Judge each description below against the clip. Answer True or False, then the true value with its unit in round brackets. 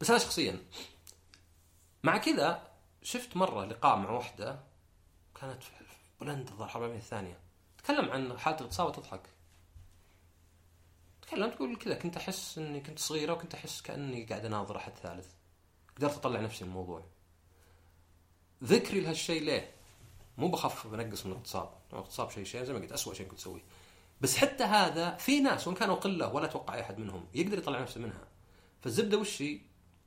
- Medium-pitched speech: False (105 Hz)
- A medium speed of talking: False (150 wpm)